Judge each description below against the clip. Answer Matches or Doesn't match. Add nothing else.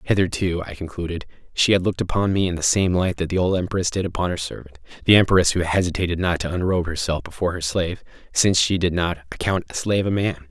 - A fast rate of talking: Matches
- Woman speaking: Doesn't match